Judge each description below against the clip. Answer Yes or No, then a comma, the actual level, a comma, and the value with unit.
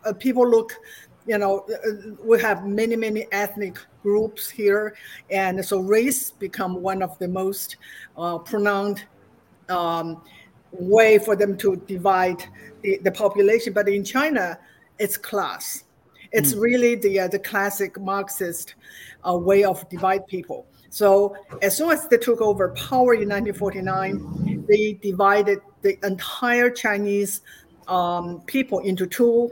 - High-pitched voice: Yes, high, 200 Hz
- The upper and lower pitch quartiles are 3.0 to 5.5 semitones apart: No, narrow, 2.4 semitones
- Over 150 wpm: No, average, 140 wpm